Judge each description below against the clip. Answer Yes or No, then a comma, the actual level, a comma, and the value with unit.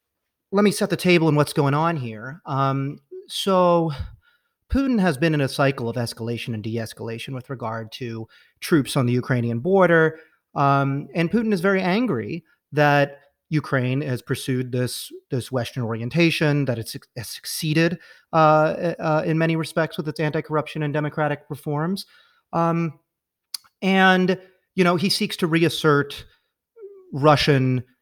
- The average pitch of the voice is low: No, medium, 155 Hz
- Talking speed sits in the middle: Yes, average, 145 wpm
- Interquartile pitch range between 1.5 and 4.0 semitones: No, average, 4.8 semitones